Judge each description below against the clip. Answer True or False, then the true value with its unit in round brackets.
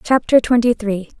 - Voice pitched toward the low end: False (230 Hz)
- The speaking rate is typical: True (150 wpm)